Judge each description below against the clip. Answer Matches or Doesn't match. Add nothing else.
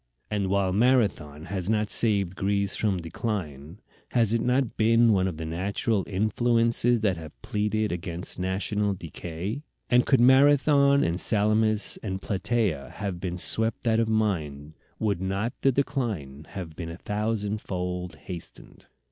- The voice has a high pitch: Doesn't match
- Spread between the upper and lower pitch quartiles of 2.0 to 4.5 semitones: Matches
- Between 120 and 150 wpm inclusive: Matches